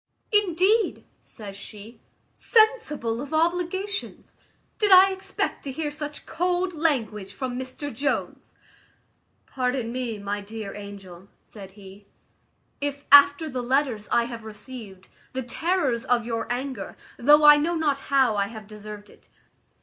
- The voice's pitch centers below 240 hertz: No, very high, 255 Hz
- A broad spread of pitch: Yes, wide, 6.2 semitones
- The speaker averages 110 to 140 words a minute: Yes, slow, 135 wpm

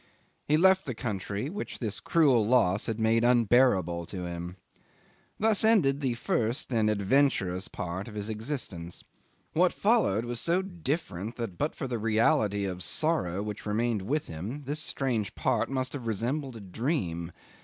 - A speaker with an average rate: Yes, average, 160 wpm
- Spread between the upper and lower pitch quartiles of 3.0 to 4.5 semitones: No, wide, 5.6 semitones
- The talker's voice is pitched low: Yes, low, 115 Hz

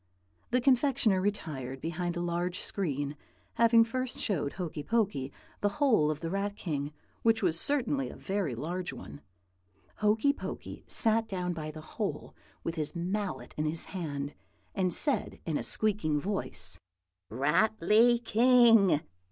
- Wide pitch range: Yes, wide, 6.4 semitones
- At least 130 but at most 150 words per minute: Yes, average, 145 wpm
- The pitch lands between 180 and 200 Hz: Yes, medium, 185 Hz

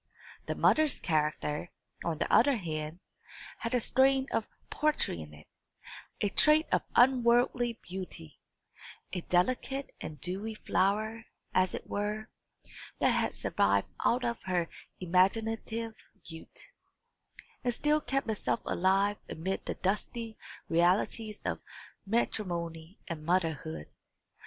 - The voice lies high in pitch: Yes, high, 200 Hz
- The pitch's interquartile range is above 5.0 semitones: Yes, wide, 5.6 semitones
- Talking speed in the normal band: No, slow, 120 wpm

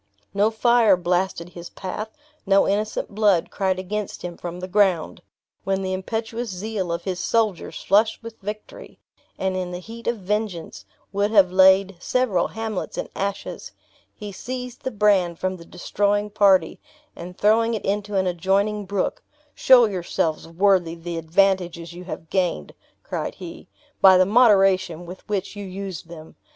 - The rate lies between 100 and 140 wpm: No, average, 160 wpm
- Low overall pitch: No, high, 195 Hz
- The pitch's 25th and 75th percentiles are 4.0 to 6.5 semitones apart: No, average, 2.7 semitones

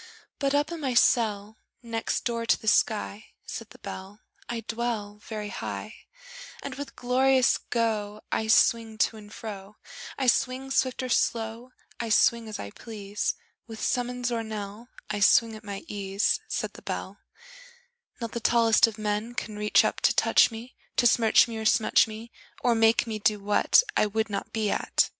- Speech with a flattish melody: Yes, narrow, 2.3 semitones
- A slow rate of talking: No, average, 180 wpm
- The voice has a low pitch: No, high, 225 Hz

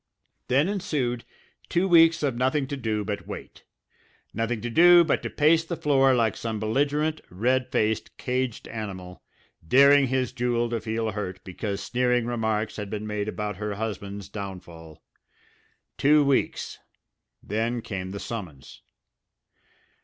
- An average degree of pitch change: Yes, average, 4.5 semitones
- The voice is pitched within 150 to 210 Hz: No, low, 115 Hz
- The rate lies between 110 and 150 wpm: Yes, average, 140 wpm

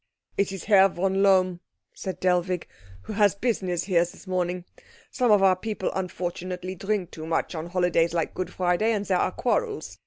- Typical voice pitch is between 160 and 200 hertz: Yes, medium, 185 Hz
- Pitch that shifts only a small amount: Yes, narrow, 2.0 semitones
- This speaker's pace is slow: No, average, 180 wpm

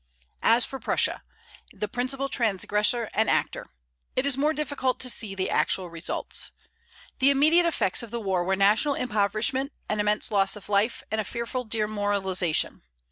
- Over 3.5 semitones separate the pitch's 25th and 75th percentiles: Yes, average, 4.4 semitones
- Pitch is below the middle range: No, high, 220 Hz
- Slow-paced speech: No, average, 160 wpm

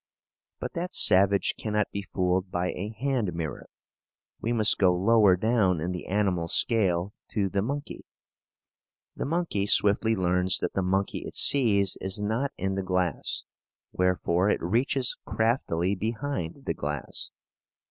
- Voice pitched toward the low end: Yes, low, 100 Hz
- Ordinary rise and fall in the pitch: Yes, average, 3.6 semitones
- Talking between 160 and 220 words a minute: No, average, 145 wpm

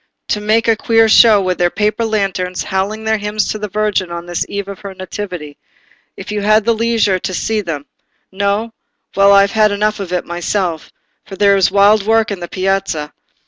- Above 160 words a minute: Yes, average, 195 wpm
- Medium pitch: No, high, 200 Hz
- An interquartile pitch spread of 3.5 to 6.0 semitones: No, narrow, 2.4 semitones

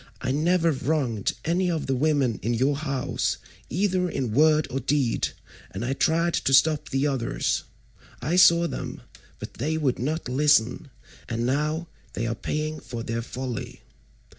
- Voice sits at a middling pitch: Yes, medium, 145 Hz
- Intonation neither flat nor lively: Yes, average, 4.1 semitones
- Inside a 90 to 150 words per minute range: No, average, 160 wpm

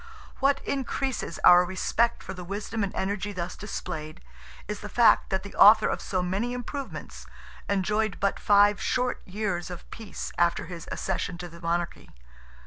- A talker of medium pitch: No, high, 200 Hz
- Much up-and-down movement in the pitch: No, average, 3.4 semitones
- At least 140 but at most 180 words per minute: Yes, average, 160 wpm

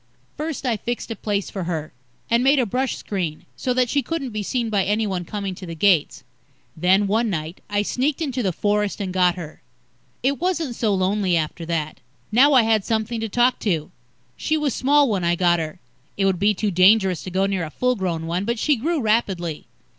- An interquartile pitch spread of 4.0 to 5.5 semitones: Yes, average, 5.1 semitones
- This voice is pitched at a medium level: No, high, 205 Hz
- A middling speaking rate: No, fast, 215 wpm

